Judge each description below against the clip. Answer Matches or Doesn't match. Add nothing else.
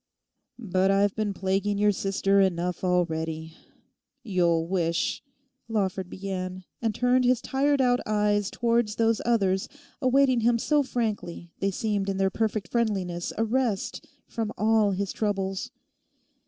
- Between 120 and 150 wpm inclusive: Matches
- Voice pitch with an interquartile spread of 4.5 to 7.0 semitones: Doesn't match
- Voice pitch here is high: Matches